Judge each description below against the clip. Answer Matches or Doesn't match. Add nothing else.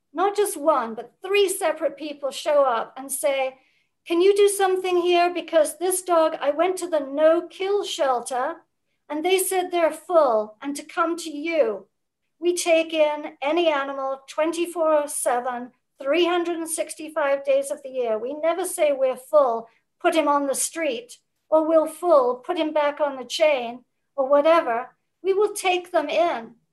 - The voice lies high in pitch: Matches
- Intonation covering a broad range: Doesn't match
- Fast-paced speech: Doesn't match